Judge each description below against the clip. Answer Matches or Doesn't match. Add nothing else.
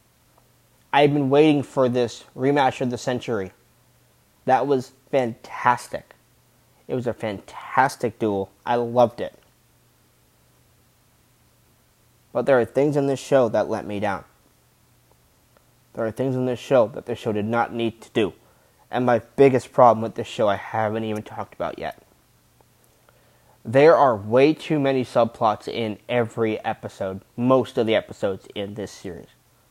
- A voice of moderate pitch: Doesn't match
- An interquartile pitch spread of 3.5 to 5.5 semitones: Doesn't match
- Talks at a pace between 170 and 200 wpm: Doesn't match